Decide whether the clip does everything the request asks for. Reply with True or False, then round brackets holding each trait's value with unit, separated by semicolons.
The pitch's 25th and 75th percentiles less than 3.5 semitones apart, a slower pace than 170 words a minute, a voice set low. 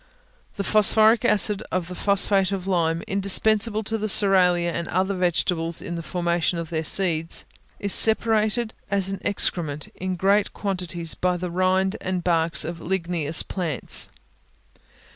False (2.7 semitones; 145 wpm; 185 Hz)